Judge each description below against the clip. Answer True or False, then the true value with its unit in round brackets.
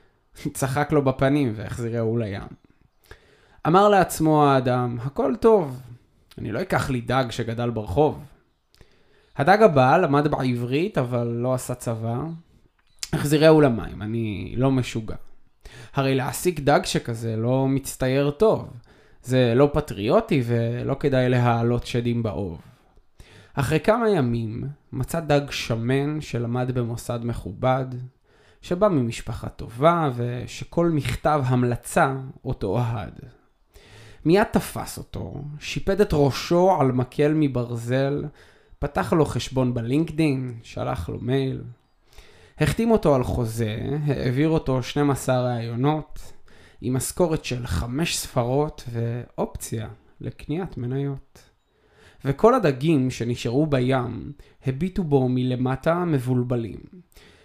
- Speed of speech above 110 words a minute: False (105 wpm)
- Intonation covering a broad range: False (3.7 semitones)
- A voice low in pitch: True (130 Hz)